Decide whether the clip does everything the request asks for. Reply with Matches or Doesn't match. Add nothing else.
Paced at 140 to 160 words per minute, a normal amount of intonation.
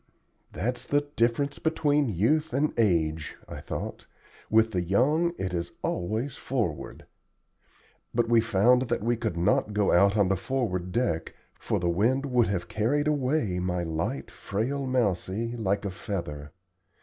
Doesn't match